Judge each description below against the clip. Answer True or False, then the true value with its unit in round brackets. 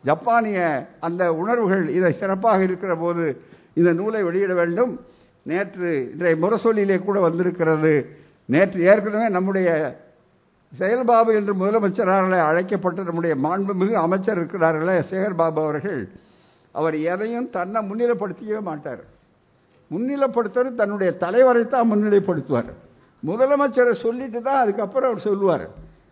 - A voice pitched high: True (195 Hz)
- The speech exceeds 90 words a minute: True (105 wpm)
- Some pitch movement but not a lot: True (4.8 semitones)